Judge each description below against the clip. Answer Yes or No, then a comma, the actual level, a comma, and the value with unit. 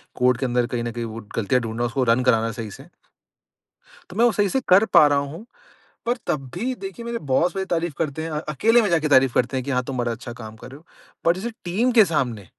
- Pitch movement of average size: No, wide, 6.9 semitones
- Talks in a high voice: No, medium, 140 Hz